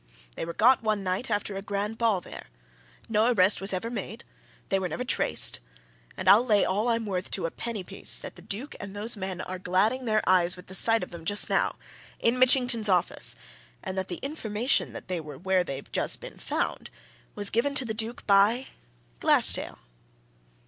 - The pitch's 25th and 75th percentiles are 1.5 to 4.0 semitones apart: Yes, average, 3.6 semitones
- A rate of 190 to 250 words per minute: Yes, average, 195 wpm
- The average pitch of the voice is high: Yes, high, 205 Hz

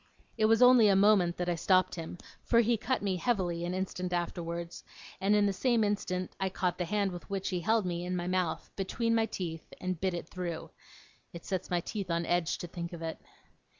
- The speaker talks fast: Yes, fast, 220 wpm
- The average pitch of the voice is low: No, medium, 185 Hz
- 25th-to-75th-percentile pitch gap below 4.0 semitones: Yes, average, 2.9 semitones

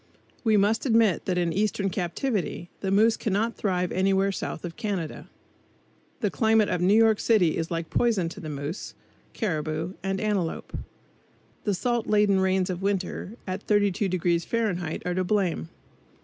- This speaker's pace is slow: No, average, 150 wpm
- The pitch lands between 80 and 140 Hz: No, high, 195 Hz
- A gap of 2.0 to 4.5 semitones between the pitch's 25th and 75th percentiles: Yes, average, 3.3 semitones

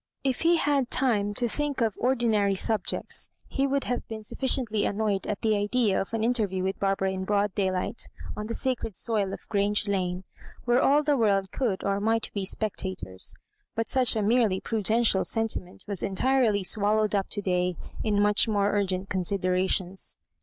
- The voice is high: Yes, high, 210 Hz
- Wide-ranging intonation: No, average, 3.2 semitones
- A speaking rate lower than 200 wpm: Yes, average, 190 wpm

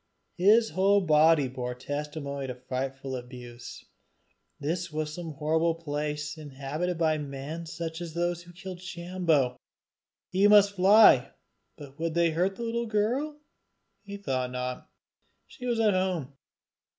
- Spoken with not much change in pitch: No, average, 4.8 semitones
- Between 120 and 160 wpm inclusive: Yes, average, 140 wpm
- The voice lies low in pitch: No, medium, 165 Hz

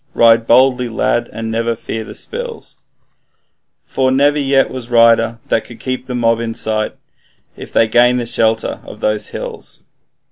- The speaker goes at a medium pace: Yes, average, 170 wpm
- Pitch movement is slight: Yes, narrow, 2.2 semitones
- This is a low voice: Yes, low, 115 Hz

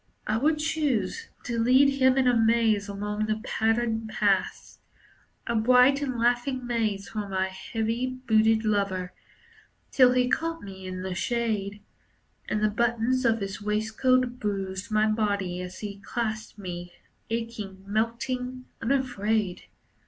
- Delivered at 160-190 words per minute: No, slow, 135 wpm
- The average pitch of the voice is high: Yes, high, 220 Hz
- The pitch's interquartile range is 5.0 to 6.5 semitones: No, average, 3.5 semitones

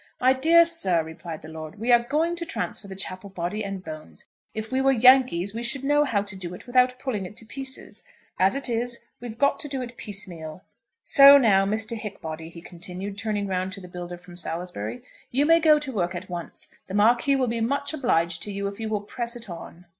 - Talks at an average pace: No, fast, 225 wpm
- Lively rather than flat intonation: Yes, wide, 6.2 semitones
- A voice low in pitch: No, high, 210 Hz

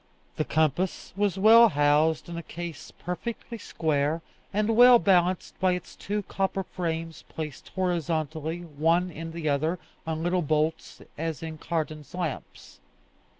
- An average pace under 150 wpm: Yes, average, 140 wpm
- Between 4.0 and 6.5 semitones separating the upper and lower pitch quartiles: No, average, 2.8 semitones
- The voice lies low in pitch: No, medium, 165 Hz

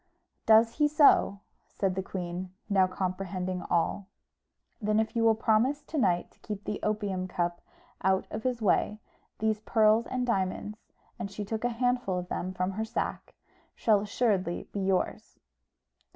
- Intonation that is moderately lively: Yes, average, 3.1 semitones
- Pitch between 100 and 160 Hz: No, high, 205 Hz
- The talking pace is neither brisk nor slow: Yes, average, 160 wpm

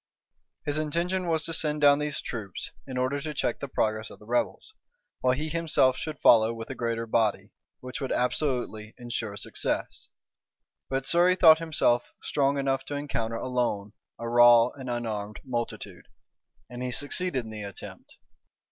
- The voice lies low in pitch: Yes, low, 125 Hz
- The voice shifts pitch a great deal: No, average, 4.3 semitones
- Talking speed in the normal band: Yes, average, 165 wpm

